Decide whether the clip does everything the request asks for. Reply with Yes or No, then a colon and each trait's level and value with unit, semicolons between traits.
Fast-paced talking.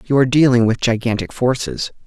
No: average, 175 wpm